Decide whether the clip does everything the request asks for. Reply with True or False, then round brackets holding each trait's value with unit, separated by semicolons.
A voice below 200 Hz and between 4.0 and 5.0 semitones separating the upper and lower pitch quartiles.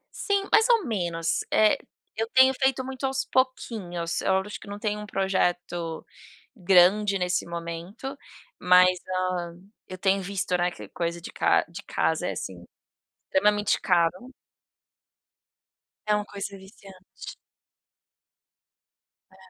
False (190 Hz; 3.3 semitones)